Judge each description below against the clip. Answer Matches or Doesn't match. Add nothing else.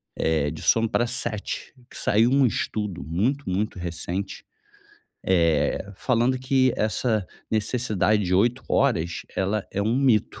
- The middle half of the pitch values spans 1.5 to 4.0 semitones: Doesn't match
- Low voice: Matches